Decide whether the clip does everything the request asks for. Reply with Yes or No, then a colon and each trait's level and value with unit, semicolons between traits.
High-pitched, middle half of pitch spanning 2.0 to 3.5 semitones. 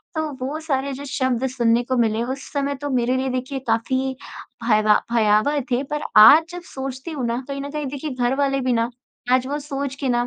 Yes: very high, 265 Hz; average, 2.8 semitones